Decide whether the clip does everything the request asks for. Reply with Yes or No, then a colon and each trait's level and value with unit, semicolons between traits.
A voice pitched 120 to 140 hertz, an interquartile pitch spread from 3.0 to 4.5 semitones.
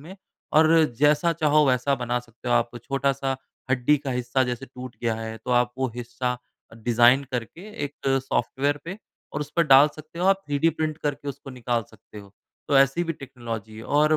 Yes: low, 135 Hz; average, 3.4 semitones